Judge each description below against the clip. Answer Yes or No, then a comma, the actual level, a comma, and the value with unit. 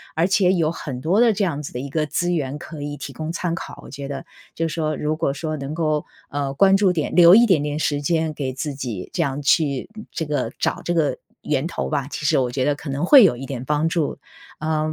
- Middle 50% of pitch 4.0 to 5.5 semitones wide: No, average, 3.2 semitones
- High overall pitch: No, medium, 150 Hz